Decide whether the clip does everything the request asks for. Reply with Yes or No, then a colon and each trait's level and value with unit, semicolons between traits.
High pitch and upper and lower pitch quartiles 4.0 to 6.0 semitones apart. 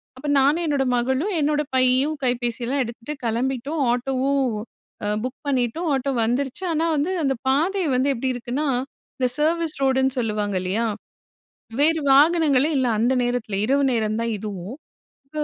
No: very high, 265 Hz; average, 3.5 semitones